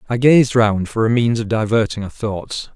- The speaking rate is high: Yes, fast, 220 wpm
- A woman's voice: No, male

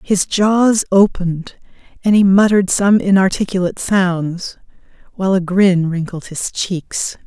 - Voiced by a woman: Yes, female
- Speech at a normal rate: No, slow, 125 wpm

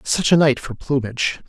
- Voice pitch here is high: No, low, 135 Hz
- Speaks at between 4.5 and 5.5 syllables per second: Yes, 5.2 syllables/s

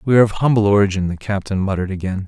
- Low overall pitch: Yes, low, 100 Hz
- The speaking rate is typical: No, fast, 235 wpm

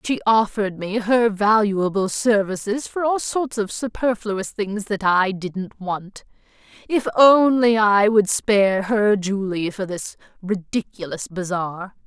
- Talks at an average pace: No, slow, 130 wpm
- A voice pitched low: No, high, 205 Hz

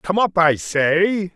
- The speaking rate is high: No, average, 180 wpm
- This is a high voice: No, medium, 175 Hz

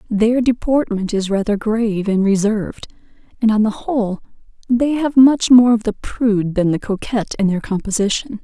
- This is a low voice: No, high, 220 Hz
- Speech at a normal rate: Yes, average, 170 wpm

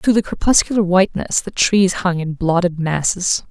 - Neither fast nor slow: Yes, average, 170 wpm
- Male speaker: No, female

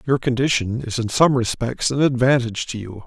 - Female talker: No, male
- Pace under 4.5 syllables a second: No, 5.4 syllables/s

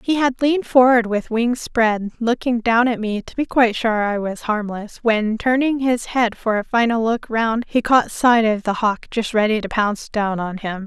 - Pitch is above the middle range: Yes, high, 225 Hz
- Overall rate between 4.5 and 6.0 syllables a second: Yes, 4.6 syllables/s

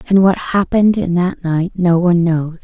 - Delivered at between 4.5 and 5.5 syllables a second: Yes, 5.0 syllables/s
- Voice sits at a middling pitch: Yes, medium, 180 Hz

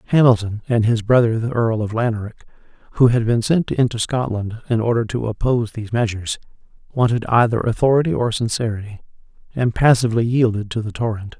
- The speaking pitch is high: No, low, 115 Hz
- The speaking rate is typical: Yes, average, 165 wpm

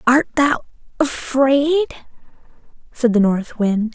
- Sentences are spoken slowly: Yes, slow, 105 wpm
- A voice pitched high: Yes, very high, 255 Hz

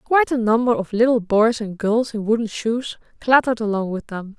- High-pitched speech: Yes, high, 225 Hz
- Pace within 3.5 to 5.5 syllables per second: Yes, 5.4 syllables/s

